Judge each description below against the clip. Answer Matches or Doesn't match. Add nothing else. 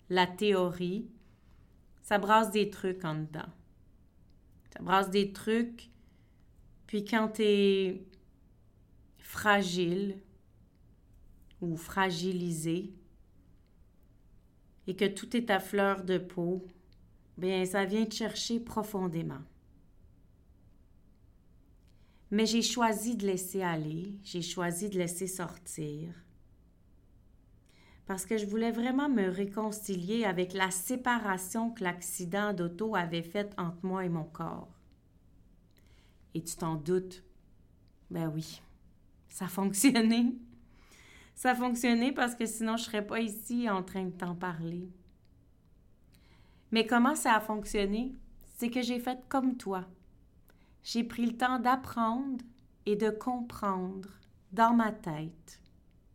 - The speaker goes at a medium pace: Doesn't match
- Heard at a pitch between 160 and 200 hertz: Matches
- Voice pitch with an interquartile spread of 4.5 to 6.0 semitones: Matches